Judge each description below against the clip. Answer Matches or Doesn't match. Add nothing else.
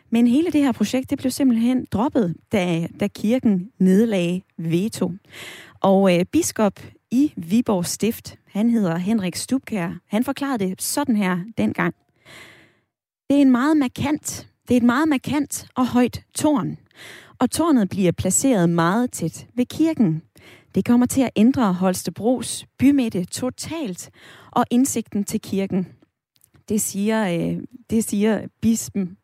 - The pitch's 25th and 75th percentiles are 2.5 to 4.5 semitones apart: Doesn't match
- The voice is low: Doesn't match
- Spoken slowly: Matches